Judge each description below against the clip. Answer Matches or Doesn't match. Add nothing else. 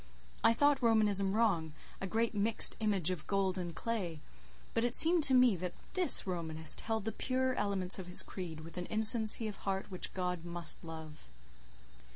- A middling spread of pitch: Matches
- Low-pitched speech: Doesn't match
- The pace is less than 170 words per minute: Doesn't match